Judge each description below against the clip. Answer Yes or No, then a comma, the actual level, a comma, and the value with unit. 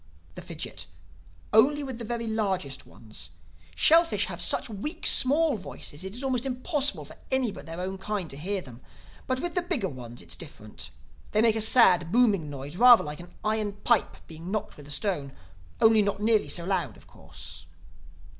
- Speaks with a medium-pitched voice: No, high, 205 Hz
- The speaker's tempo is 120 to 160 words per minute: No, average, 185 wpm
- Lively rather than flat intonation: Yes, wide, 7.1 semitones